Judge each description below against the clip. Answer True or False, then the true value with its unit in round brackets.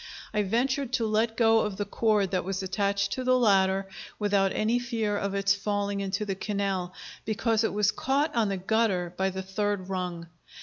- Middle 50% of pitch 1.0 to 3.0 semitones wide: True (2.5 semitones)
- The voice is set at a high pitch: True (205 Hz)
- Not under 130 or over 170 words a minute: False (190 wpm)